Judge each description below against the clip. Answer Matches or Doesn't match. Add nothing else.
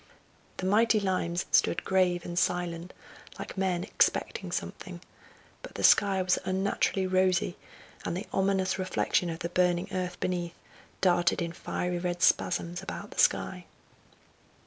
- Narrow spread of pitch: Matches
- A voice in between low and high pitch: Matches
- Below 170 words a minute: Matches